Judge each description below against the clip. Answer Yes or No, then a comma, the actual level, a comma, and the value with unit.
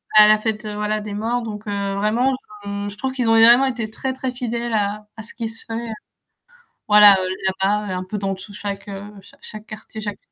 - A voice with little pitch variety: Yes, narrow, 2.0 semitones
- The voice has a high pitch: Yes, high, 215 Hz